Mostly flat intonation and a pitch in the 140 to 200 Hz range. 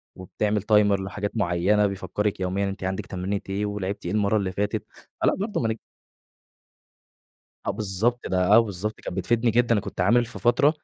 No: narrow, 2.2 semitones; low, 105 Hz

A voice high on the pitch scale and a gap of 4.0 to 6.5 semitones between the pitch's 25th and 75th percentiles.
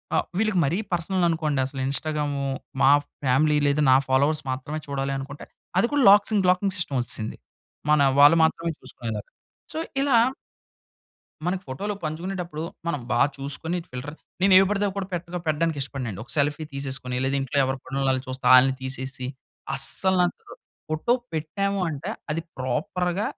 No: medium, 150 Hz; average, 4.9 semitones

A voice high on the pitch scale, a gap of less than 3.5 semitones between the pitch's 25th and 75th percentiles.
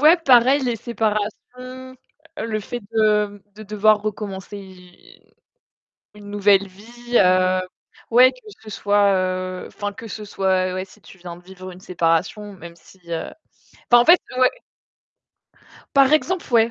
No: high, 205 Hz; average, 4.0 semitones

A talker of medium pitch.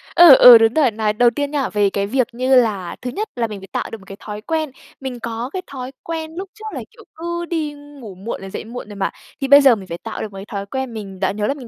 No: high, 240 Hz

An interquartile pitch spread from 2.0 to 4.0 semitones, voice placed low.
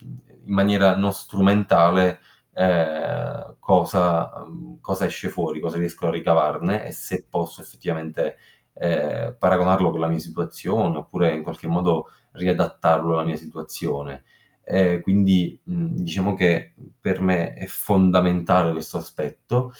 Yes: average, 2.7 semitones; very low, 90 Hz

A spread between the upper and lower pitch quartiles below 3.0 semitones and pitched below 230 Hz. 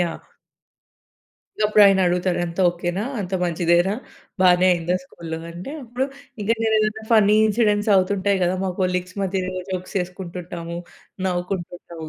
Yes: narrow, 2.4 semitones; medium, 185 Hz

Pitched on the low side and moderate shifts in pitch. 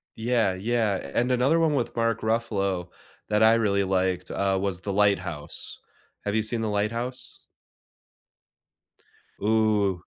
Yes: low, 105 Hz; average, 3.0 semitones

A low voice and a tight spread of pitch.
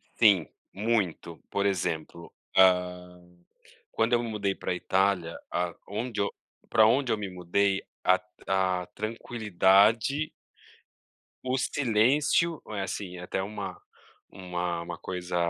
No: very low, 95 Hz; average, 3.7 semitones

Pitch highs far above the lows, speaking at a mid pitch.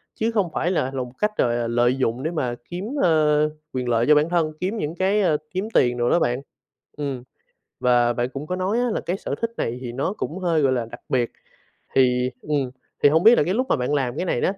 Yes: wide, 6.4 semitones; medium, 150 Hz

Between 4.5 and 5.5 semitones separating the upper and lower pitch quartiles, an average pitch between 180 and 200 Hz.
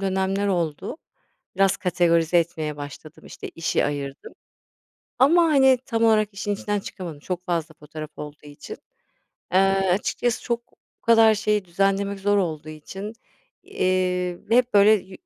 No: average, 4.0 semitones; high, 190 Hz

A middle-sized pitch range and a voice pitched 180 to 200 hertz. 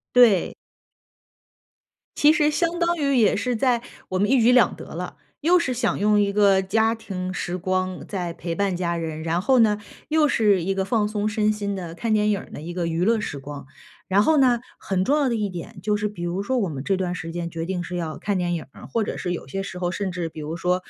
Yes: average, 4.2 semitones; high, 195 Hz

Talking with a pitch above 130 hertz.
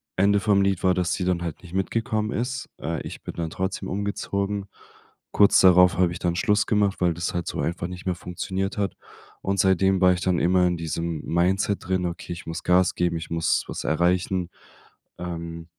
No: very low, 90 Hz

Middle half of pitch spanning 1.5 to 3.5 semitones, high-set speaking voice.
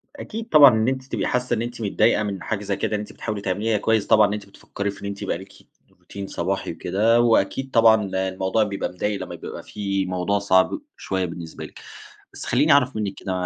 No: average, 2.8 semitones; low, 105 Hz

